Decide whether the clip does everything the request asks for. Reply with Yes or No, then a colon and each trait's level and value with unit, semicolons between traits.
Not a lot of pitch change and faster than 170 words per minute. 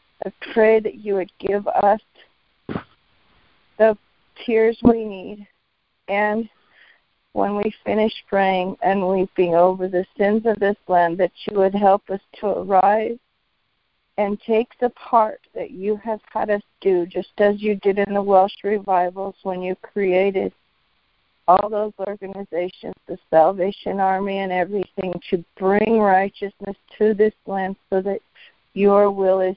No: narrow, 2.0 semitones; average, 145 wpm